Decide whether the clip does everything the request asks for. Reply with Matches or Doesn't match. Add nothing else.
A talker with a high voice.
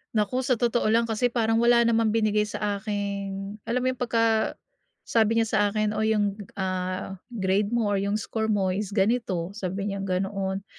Matches